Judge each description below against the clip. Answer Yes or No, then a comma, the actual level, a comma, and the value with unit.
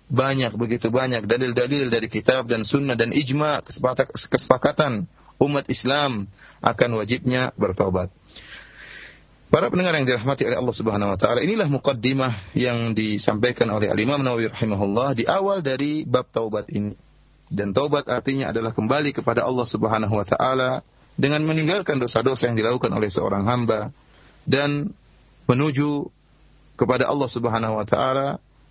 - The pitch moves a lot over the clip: No, average, 3.6 semitones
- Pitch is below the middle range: Yes, low, 125 Hz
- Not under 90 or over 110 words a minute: No, average, 135 wpm